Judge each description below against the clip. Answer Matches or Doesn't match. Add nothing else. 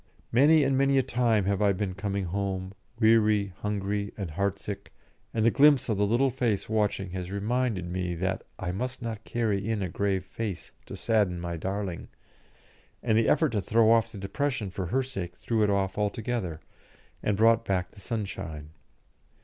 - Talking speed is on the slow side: Doesn't match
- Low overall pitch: Matches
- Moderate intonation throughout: Matches